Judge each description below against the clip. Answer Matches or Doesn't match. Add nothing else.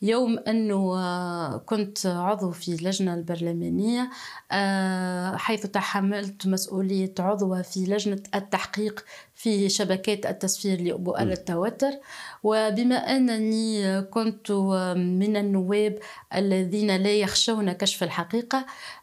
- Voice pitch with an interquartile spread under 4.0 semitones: Matches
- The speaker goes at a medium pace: Matches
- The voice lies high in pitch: Matches